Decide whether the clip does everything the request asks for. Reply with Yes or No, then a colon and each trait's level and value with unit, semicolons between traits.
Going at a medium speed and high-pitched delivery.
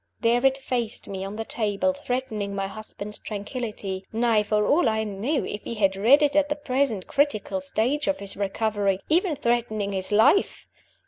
Yes: average, 175 wpm; high, 225 Hz